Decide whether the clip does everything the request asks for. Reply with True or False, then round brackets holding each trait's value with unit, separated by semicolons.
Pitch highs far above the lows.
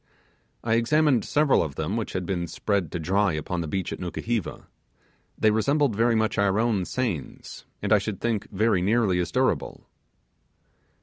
False (4.3 semitones)